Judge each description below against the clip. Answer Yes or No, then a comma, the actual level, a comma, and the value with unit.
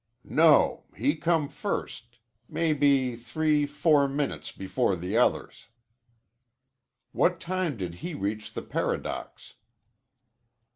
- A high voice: No, medium, 140 Hz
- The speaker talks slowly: Yes, slow, 100 wpm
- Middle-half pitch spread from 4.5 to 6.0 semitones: Yes, average, 5.0 semitones